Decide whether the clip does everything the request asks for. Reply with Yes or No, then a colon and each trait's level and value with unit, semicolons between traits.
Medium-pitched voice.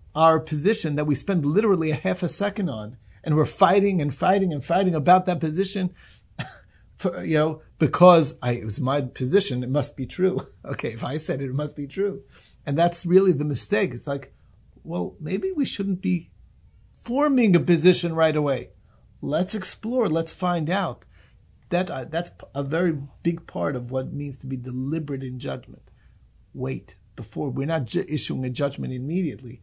Yes: medium, 155 Hz